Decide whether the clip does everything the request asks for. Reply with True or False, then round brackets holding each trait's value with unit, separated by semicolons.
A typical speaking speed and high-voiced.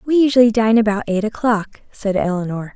True (175 wpm; 215 Hz)